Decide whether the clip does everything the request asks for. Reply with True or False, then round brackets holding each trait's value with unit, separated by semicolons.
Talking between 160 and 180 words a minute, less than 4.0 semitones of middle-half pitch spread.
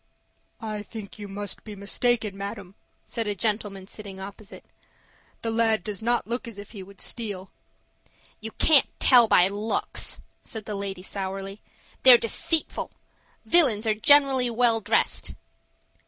False (140 wpm; 2.7 semitones)